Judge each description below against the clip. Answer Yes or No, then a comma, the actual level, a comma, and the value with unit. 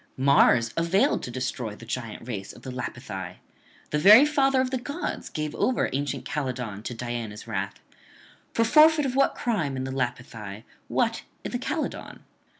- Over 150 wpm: Yes, average, 160 wpm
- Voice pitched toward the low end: Yes, low, 130 Hz